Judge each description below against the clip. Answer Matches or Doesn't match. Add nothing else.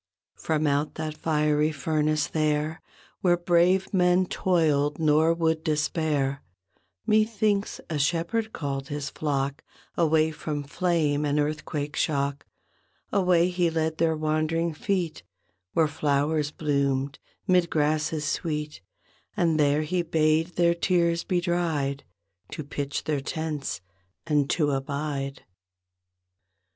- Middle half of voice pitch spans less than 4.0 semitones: Matches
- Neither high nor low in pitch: Matches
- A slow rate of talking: Matches